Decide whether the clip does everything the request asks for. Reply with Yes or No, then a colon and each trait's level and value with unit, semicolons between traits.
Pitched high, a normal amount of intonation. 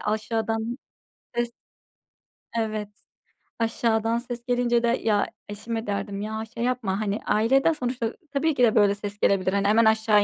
No: high, 225 Hz; narrow, 2.3 semitones